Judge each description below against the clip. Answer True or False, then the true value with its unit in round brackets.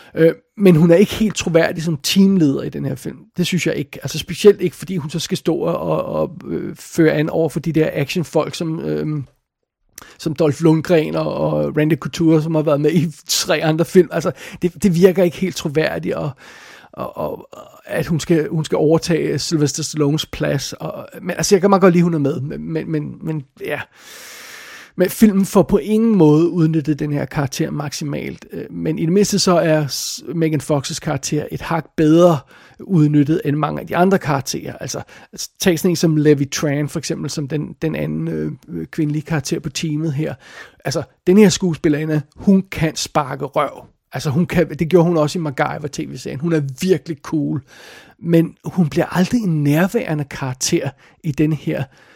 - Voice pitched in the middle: True (160 Hz)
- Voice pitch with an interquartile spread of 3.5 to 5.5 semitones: False (2.6 semitones)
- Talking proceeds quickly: False (190 wpm)